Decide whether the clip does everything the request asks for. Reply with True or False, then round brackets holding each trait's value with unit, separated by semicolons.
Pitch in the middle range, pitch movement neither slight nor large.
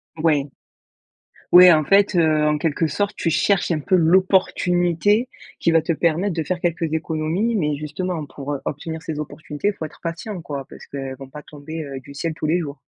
True (160 Hz; 3.0 semitones)